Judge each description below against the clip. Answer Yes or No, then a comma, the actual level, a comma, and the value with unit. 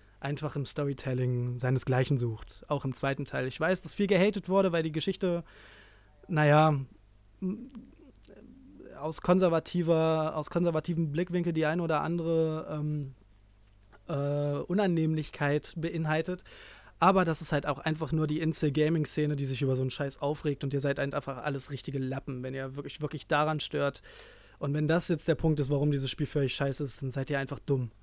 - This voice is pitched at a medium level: Yes, medium, 150 Hz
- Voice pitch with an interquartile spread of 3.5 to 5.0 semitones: No, average, 2.9 semitones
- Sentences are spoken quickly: No, average, 170 wpm